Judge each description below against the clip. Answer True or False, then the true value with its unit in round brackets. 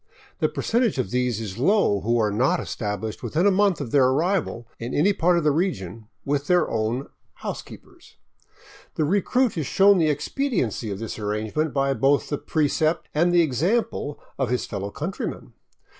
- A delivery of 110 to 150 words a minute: False (175 wpm)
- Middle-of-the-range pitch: True (145 Hz)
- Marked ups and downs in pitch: True (7.4 semitones)